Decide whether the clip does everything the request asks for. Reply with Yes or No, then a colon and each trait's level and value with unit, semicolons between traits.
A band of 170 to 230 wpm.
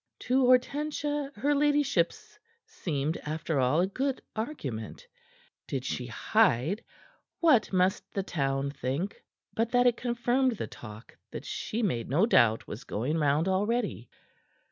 No: slow, 135 wpm